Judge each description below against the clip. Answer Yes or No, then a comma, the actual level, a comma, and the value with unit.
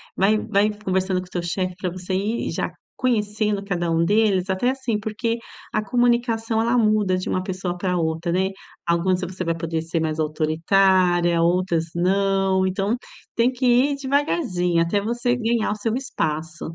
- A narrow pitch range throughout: No, average, 4.0 semitones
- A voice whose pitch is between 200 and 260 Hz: No, high, 190 Hz